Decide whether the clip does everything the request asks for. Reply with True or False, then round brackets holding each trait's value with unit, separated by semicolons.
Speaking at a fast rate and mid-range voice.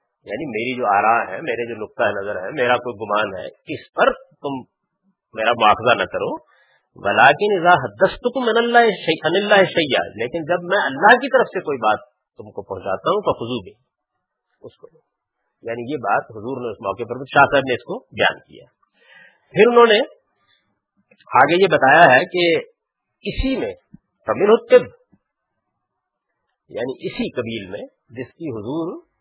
False (145 wpm; 180 Hz)